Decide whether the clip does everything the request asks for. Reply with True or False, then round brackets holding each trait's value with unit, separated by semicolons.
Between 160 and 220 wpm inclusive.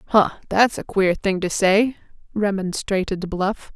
False (145 wpm)